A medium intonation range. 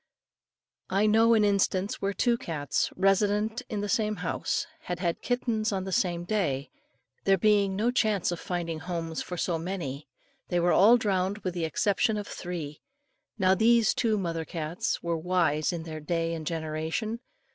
Yes: average, 4.1 semitones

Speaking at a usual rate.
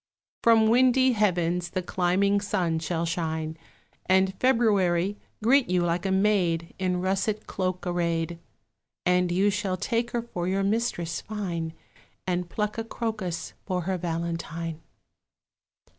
No: slow, 130 wpm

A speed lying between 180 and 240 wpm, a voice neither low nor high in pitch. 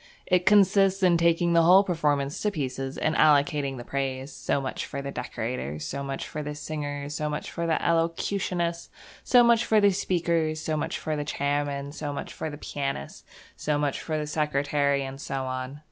Yes: average, 190 wpm; medium, 150 Hz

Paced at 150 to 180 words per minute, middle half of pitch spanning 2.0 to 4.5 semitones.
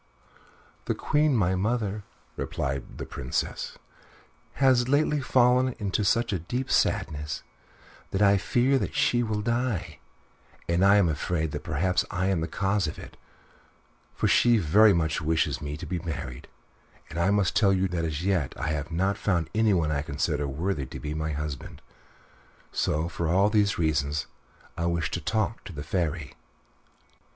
No: average, 165 wpm; average, 5.3 semitones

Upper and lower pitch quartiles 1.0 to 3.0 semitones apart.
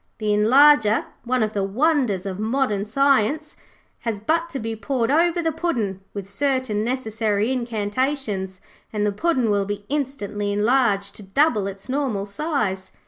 No: average, 5.1 semitones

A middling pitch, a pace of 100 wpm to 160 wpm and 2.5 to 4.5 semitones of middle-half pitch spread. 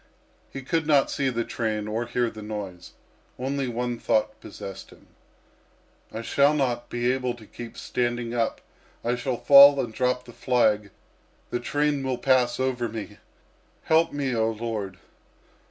No: low, 120 Hz; average, 155 wpm; average, 2.8 semitones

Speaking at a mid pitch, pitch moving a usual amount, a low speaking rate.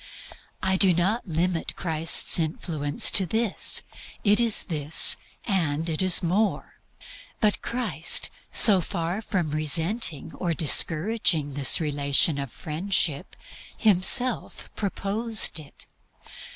Yes: medium, 175 Hz; average, 4.7 semitones; slow, 110 wpm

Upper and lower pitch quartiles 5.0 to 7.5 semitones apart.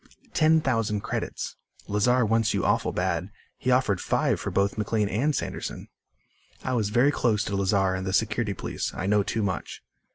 No: average, 3.5 semitones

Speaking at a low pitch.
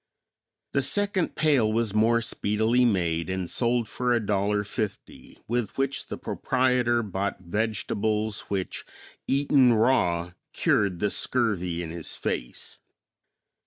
Yes: low, 110 Hz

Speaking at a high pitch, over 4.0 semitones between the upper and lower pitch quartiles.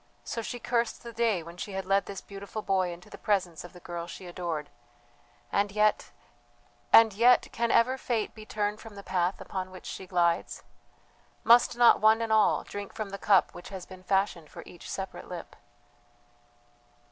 No: high, 200 Hz; average, 3.4 semitones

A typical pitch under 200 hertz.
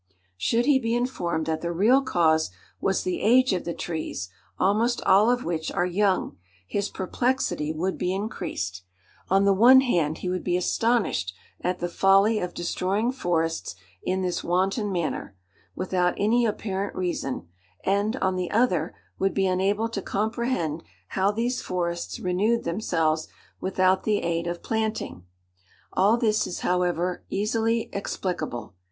Yes: high, 190 Hz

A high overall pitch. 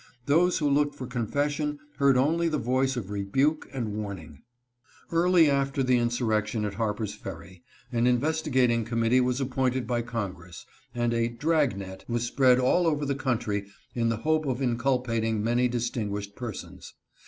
No: low, 125 Hz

